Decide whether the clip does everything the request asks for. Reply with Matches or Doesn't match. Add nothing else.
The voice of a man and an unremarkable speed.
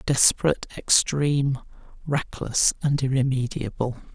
Doesn't match